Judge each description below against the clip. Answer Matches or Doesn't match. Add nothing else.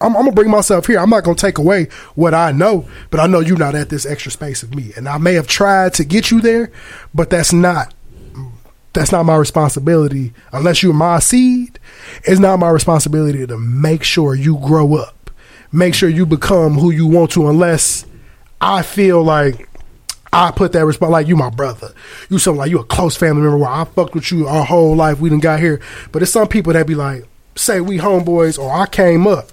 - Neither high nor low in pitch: Matches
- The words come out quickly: Matches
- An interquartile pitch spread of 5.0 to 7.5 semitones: Doesn't match